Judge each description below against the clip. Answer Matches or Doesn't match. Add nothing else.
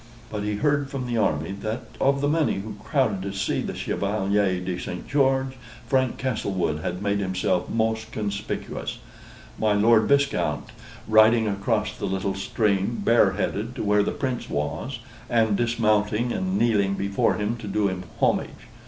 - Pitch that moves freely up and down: Doesn't match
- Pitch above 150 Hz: Doesn't match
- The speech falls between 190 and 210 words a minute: Doesn't match